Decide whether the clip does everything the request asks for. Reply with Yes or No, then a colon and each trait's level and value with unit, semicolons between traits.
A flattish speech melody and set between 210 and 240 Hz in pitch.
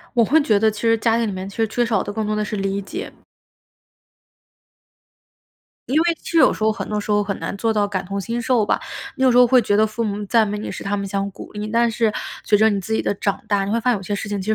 Yes: narrow, 2.2 semitones; high, 215 Hz